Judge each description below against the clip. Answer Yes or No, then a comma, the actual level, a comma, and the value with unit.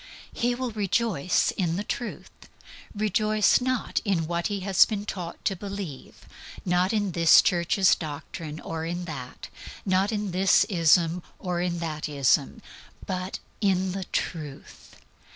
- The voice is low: No, medium, 185 Hz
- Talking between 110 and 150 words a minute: Yes, average, 140 wpm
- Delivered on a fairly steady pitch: No, average, 3.4 semitones